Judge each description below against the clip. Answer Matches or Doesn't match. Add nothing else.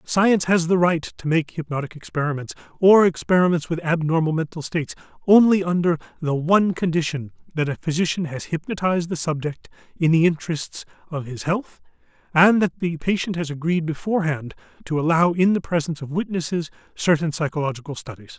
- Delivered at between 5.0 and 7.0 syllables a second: Matches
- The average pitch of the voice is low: Doesn't match